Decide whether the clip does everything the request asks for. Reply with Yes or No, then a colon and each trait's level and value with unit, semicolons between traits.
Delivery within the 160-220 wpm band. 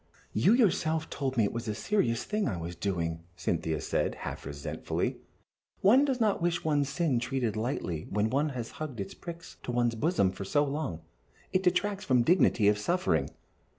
Yes: average, 185 wpm